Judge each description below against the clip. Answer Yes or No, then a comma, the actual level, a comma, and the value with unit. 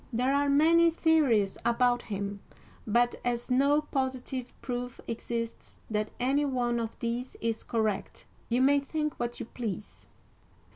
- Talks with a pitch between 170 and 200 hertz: No, high, 245 Hz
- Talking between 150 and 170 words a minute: No, average, 140 wpm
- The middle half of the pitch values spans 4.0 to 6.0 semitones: No, average, 3.2 semitones